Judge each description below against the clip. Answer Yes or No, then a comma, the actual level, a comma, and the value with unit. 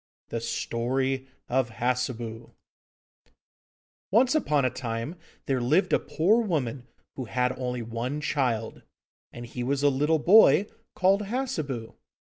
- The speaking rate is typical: No, slow, 130 wpm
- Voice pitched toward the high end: No, low, 130 Hz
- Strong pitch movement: No, average, 4.5 semitones